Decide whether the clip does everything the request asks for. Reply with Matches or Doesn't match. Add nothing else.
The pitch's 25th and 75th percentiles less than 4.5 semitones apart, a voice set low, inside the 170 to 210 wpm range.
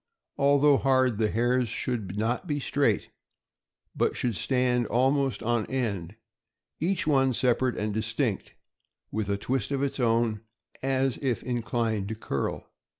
Doesn't match